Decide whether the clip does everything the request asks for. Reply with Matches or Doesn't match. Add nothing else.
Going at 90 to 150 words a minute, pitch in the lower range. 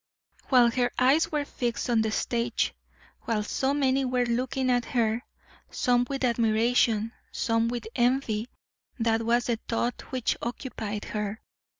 Doesn't match